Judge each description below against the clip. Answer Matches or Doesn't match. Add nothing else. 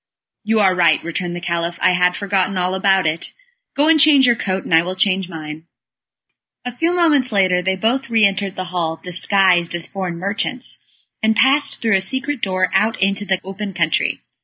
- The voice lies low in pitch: Doesn't match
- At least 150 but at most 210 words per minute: Matches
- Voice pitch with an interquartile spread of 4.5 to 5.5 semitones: Doesn't match